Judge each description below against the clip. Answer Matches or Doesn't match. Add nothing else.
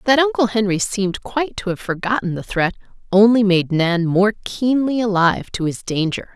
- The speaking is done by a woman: Matches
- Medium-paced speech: Matches